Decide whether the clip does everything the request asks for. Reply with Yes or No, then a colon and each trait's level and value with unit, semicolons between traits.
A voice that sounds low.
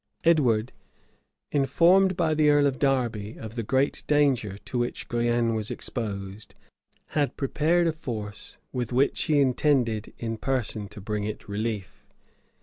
Yes: low, 120 Hz